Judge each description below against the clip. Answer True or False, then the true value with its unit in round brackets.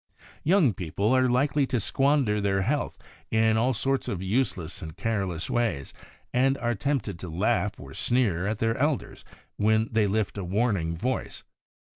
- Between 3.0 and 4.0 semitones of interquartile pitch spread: False (4.9 semitones)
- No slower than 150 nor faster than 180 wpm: True (160 wpm)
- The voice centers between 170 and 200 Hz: False (110 Hz)